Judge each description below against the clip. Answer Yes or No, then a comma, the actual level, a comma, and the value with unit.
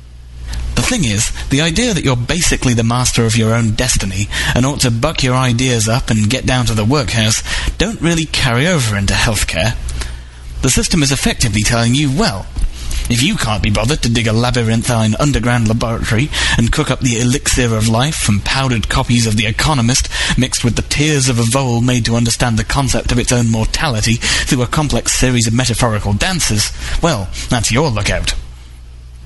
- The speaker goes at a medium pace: Yes, average, 185 wpm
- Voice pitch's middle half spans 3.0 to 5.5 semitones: Yes, average, 3.3 semitones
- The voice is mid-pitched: No, low, 120 Hz